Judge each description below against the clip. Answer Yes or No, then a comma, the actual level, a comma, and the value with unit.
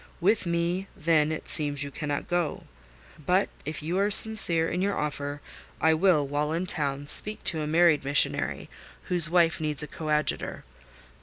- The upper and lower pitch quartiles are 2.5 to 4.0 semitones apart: Yes, average, 3.0 semitones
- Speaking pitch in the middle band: Yes, medium, 160 Hz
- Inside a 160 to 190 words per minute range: Yes, average, 165 wpm